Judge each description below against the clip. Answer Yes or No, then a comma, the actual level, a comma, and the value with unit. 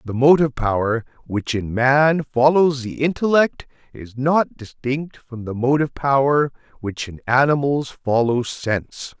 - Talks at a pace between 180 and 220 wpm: No, average, 145 wpm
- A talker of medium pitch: No, low, 130 Hz